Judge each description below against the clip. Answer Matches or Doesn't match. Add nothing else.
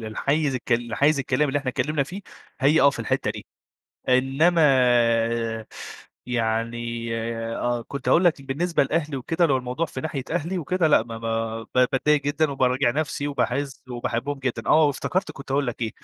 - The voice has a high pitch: Doesn't match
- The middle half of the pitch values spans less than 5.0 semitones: Matches